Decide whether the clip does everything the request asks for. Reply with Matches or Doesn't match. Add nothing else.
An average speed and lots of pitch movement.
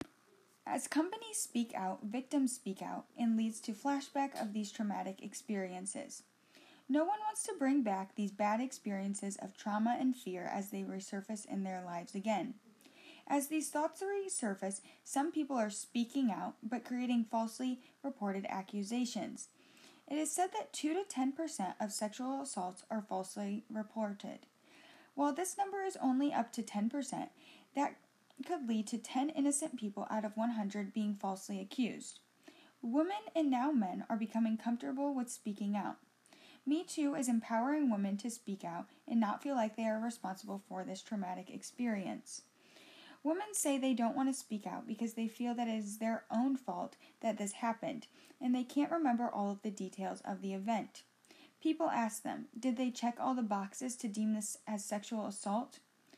Doesn't match